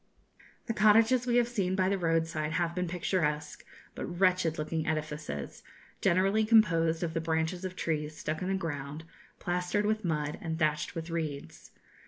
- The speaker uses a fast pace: No, average, 165 wpm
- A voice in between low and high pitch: Yes, medium, 165 Hz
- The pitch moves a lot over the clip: No, average, 3.2 semitones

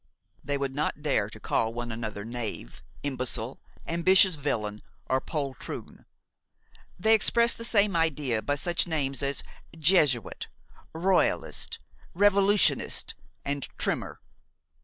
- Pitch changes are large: Yes, wide, 6.7 semitones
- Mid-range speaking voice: Yes, medium, 145 Hz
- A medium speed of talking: No, slow, 115 wpm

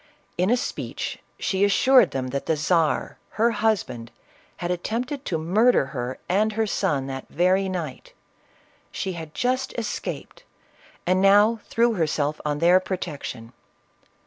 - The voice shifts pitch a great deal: Yes, wide, 6.3 semitones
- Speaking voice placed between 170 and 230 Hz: Yes, medium, 185 Hz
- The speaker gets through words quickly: No, average, 145 wpm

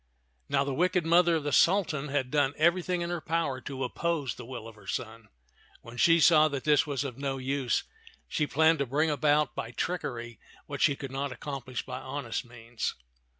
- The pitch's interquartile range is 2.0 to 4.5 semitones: Yes, average, 3.8 semitones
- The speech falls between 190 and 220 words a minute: Yes, average, 200 wpm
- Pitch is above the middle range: No, medium, 140 Hz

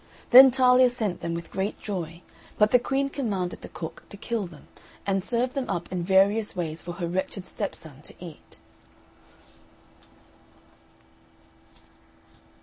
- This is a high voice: Yes, high, 195 Hz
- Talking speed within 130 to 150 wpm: Yes, average, 140 wpm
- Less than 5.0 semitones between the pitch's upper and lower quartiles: No, wide, 5.6 semitones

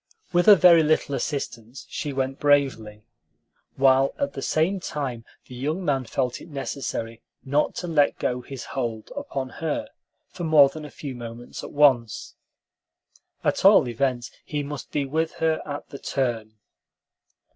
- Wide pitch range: No, average, 3.6 semitones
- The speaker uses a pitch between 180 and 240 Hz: No, medium, 140 Hz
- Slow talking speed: No, average, 155 wpm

